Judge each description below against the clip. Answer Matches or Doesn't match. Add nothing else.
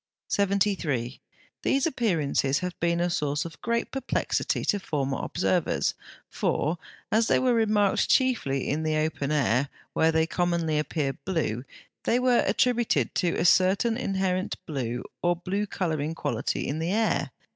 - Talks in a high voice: Doesn't match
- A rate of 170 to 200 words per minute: Doesn't match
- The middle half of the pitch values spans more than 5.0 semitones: Matches